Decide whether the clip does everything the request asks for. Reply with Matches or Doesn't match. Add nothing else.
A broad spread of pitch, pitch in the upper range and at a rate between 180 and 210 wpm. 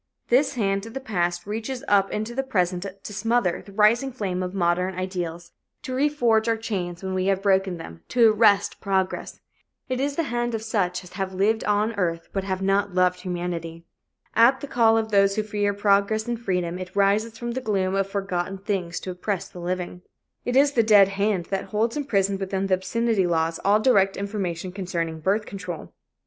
Doesn't match